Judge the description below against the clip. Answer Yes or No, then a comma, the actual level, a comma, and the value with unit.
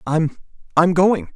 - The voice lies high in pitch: No, medium, 160 Hz